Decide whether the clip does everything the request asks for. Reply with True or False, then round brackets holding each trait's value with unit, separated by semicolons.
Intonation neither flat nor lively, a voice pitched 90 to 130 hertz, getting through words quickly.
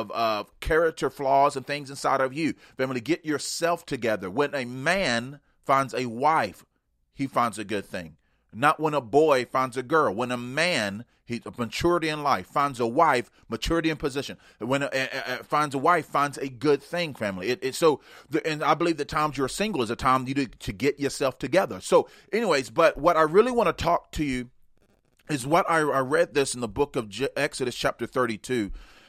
False (3.7 semitones; 140 Hz; 210 wpm)